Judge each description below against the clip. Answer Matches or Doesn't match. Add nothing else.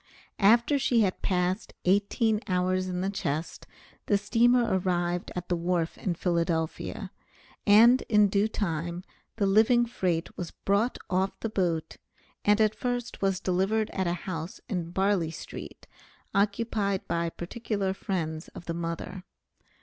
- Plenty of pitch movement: Doesn't match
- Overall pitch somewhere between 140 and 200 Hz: Matches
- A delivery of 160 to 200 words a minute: Doesn't match